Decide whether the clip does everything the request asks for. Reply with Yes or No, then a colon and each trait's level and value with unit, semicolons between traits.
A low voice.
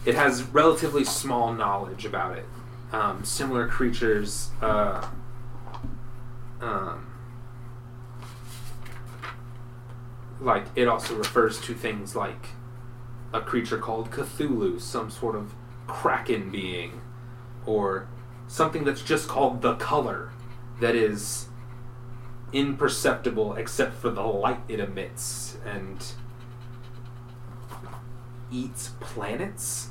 Yes: low, 120 Hz